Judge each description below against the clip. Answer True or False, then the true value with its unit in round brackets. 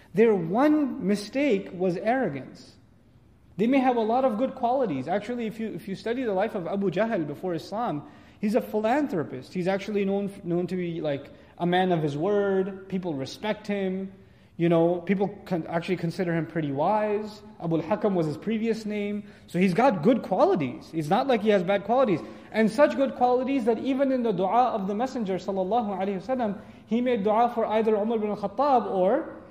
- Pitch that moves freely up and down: False (4.3 semitones)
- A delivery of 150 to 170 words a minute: False (190 wpm)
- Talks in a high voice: True (205 Hz)